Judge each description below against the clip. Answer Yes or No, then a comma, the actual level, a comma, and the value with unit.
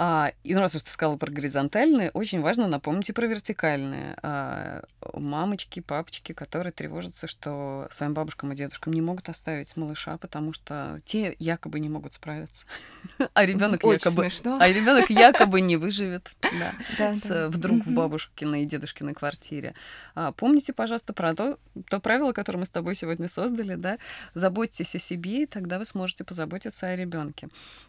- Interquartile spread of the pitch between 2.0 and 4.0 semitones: No, average, 5.1 semitones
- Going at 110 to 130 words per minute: No, average, 145 wpm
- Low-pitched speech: No, medium, 175 Hz